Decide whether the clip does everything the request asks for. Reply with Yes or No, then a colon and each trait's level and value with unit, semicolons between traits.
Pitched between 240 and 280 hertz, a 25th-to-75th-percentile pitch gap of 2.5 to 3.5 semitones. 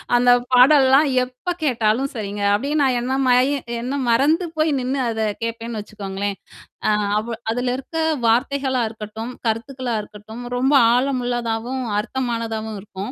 Yes: high, 245 Hz; average, 3.0 semitones